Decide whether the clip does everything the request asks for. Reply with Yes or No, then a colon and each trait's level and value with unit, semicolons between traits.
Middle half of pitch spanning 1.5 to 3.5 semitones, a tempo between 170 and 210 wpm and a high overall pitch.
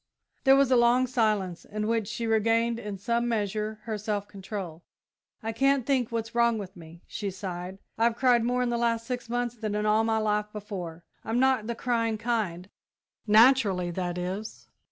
Yes: average, 2.7 semitones; average, 185 wpm; high, 220 Hz